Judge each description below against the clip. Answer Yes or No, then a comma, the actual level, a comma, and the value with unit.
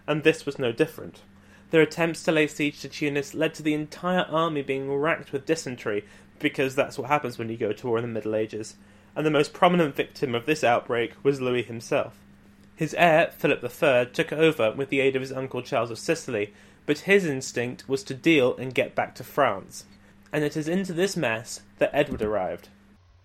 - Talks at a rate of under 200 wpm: No, fast, 205 wpm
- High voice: No, low, 135 Hz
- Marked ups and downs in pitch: Yes, wide, 6.1 semitones